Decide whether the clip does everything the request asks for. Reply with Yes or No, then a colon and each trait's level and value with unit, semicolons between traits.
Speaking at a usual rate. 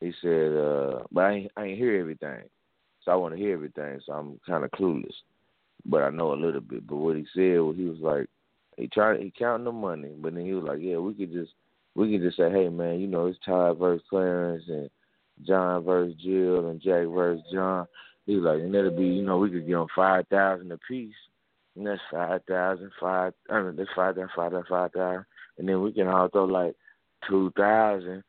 No: fast, 225 wpm